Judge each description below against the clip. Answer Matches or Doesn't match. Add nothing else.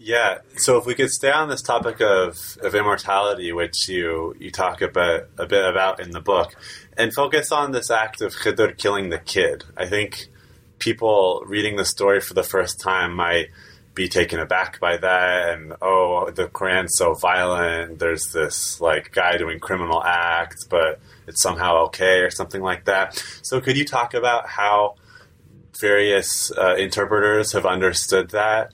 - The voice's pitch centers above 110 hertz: Doesn't match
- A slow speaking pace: Doesn't match